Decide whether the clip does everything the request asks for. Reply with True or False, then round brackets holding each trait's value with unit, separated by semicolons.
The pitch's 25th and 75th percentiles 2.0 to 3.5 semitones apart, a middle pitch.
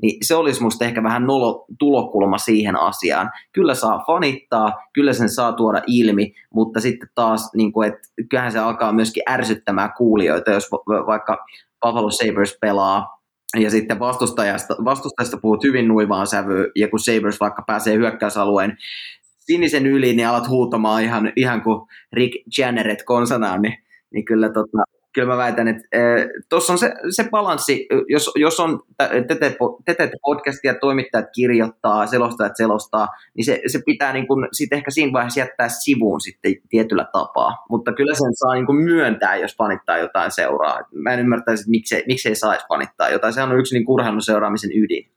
False (3.2 semitones; 115 Hz)